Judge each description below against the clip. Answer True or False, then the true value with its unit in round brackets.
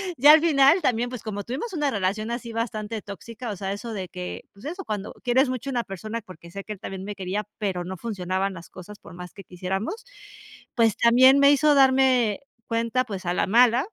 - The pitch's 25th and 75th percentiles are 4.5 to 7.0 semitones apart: True (4.8 semitones)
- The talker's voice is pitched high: True (225 Hz)